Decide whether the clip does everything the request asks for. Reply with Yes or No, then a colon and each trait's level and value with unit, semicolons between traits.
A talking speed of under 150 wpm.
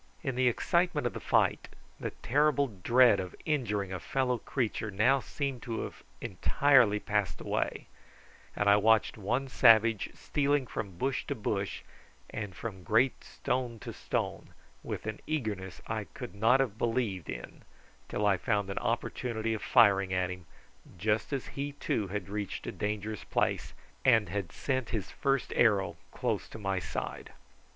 No: average, 160 wpm